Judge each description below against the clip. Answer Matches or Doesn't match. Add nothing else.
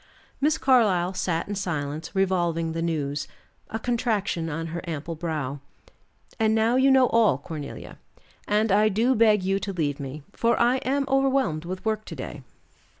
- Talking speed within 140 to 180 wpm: Matches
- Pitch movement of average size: Doesn't match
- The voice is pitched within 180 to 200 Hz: Matches